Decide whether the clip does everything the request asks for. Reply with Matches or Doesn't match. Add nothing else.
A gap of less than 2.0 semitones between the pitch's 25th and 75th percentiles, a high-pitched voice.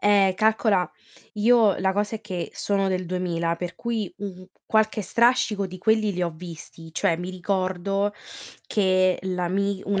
Doesn't match